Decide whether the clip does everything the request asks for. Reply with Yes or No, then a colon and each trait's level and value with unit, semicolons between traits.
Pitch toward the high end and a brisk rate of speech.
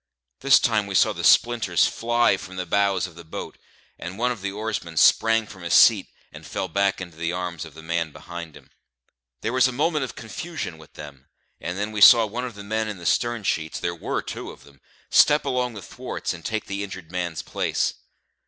No: low, 100 Hz; fast, 220 wpm